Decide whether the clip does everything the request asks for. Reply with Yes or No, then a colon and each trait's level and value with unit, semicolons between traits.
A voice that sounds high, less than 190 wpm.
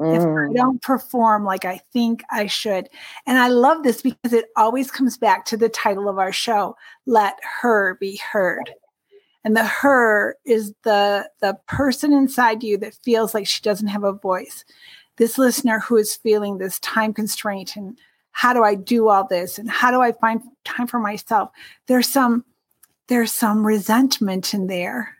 Yes: high, 225 Hz; average, 180 wpm